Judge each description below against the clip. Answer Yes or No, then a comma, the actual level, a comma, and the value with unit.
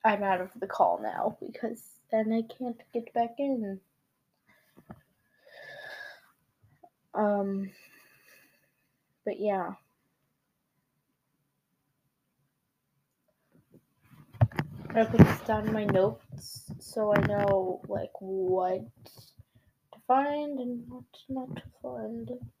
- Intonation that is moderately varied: No, wide, 7.1 semitones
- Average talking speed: No, slow, 95 wpm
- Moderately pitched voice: No, high, 200 Hz